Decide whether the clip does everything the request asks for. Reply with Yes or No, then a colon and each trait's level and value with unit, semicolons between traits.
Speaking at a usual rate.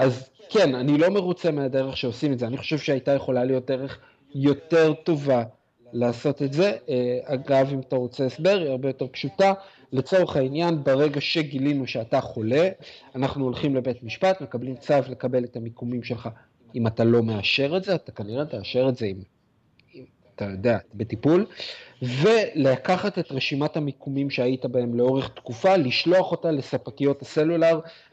No: fast, 155 wpm